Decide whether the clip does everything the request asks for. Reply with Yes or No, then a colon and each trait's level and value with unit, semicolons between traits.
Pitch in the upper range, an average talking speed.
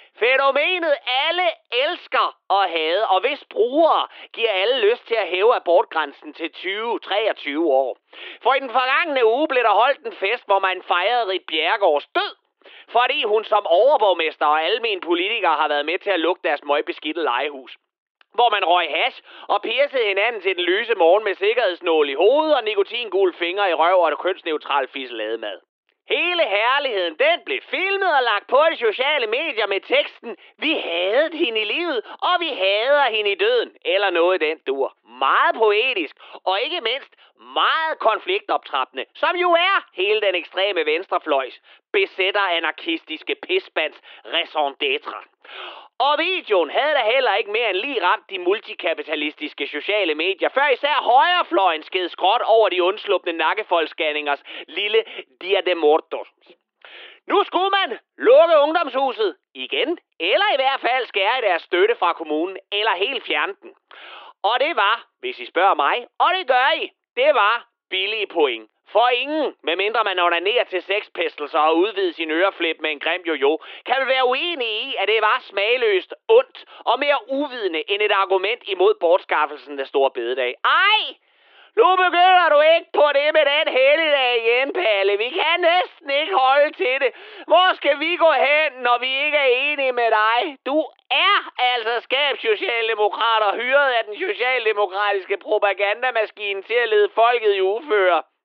Yes: very high, 320 Hz; average, 160 wpm